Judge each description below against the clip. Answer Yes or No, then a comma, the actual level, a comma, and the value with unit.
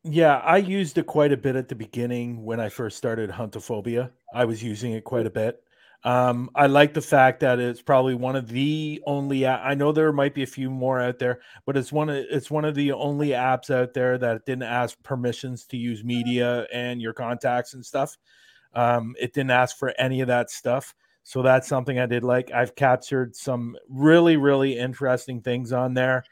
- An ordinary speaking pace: No, fast, 210 wpm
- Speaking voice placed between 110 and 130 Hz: Yes, low, 125 Hz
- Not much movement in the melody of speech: Yes, narrow, 2.3 semitones